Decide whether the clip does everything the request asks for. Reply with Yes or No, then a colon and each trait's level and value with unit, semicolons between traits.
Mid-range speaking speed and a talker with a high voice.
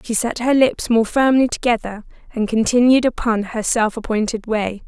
Yes: average, 170 wpm; high, 230 Hz